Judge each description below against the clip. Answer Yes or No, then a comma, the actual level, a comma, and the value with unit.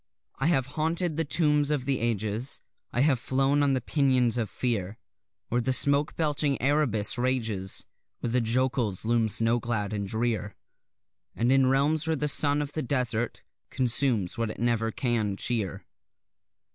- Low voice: Yes, low, 125 Hz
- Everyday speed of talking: Yes, average, 160 wpm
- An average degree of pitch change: Yes, average, 3.9 semitones